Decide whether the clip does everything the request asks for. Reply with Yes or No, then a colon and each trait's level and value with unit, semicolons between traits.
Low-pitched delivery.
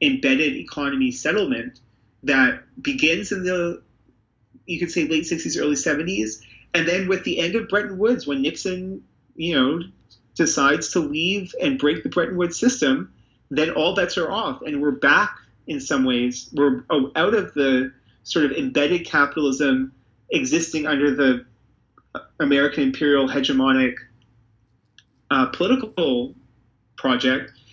No: medium, 145 Hz